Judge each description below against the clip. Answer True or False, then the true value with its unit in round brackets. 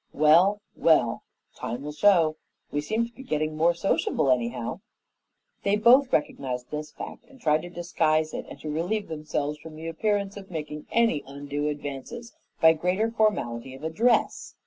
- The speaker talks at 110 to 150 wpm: False (165 wpm)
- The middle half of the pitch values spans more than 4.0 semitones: True (5.4 semitones)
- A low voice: False (160 Hz)